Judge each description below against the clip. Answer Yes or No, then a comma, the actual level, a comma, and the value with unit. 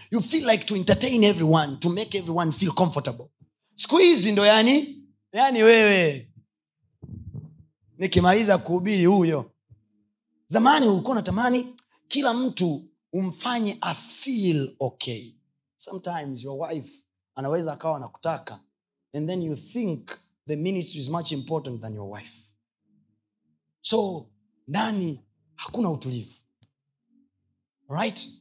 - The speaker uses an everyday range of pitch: No, wide, 8.4 semitones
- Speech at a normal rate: Yes, average, 110 wpm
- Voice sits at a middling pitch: Yes, medium, 160 Hz